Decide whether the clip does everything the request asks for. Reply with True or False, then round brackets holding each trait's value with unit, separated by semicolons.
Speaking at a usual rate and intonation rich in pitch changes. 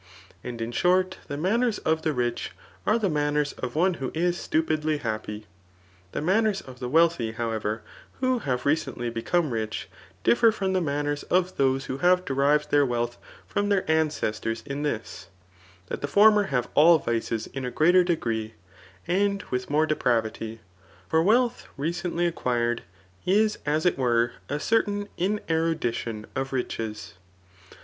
True (155 wpm; 6.8 semitones)